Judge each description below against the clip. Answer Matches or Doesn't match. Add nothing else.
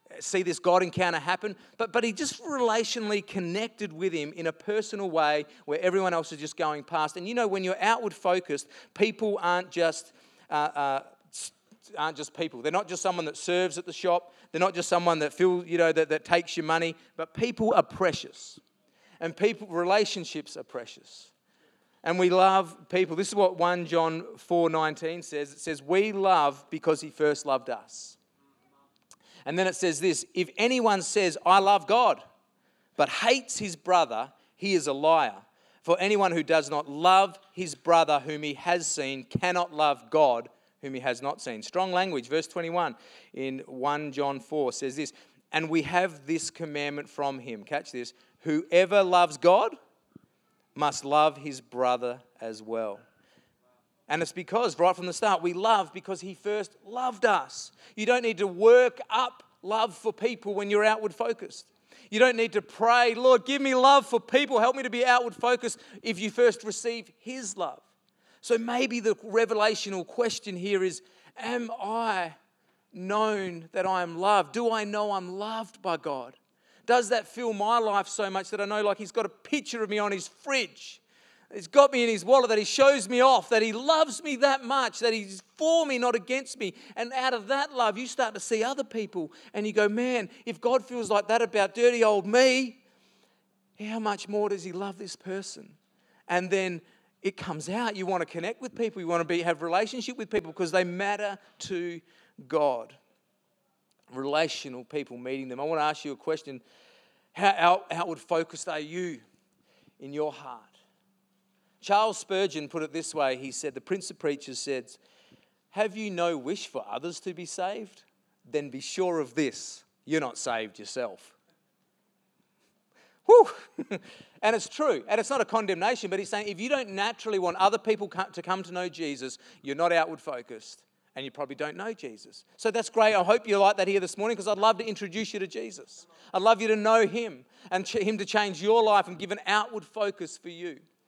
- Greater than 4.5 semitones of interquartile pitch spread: Matches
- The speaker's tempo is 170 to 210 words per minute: Matches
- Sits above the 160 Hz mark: Matches